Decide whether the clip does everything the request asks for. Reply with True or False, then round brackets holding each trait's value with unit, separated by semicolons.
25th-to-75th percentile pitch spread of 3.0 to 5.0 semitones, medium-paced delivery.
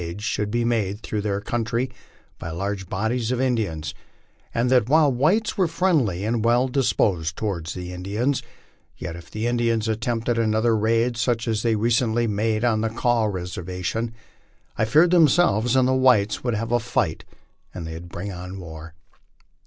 True (3.6 semitones; 180 wpm)